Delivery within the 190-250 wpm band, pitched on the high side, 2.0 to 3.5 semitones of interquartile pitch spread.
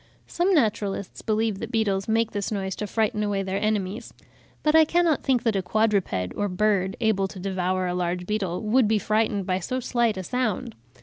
Yes: average, 195 wpm; high, 210 Hz; average, 2.8 semitones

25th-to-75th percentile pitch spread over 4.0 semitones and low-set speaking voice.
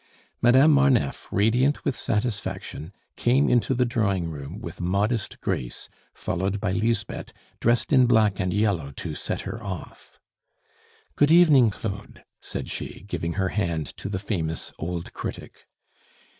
Yes: average, 5.2 semitones; low, 105 Hz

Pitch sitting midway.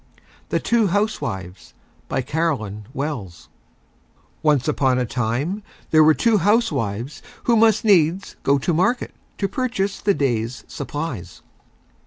Yes: medium, 150 Hz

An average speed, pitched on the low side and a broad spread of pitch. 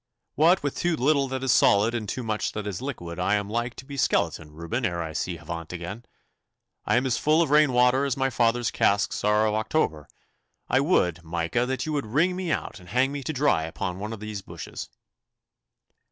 No: fast, 215 wpm; low, 115 Hz; wide, 6.8 semitones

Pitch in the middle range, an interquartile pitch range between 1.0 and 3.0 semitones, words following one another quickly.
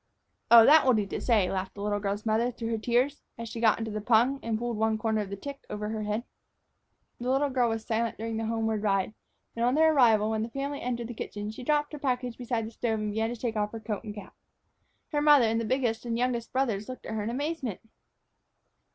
No: high, 230 Hz; narrow, 2.4 semitones; fast, 250 wpm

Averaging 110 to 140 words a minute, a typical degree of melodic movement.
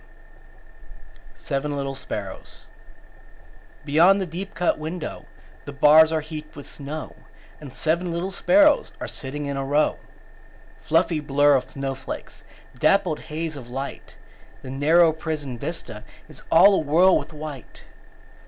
Yes: slow, 135 wpm; average, 3.0 semitones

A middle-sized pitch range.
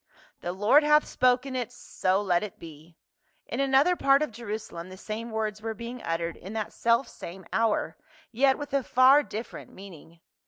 No: wide, 5.7 semitones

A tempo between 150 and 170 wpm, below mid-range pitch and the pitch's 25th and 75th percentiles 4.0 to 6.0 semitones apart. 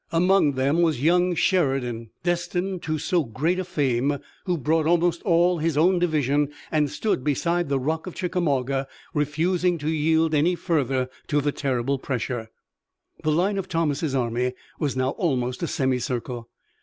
No: average, 155 wpm; medium, 150 Hz; average, 4.4 semitones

